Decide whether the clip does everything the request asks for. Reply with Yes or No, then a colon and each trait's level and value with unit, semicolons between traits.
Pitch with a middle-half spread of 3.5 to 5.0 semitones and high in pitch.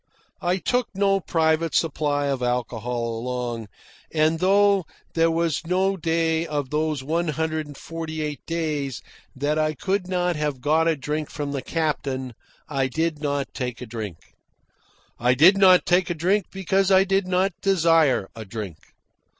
No: average, 4.3 semitones; medium, 155 Hz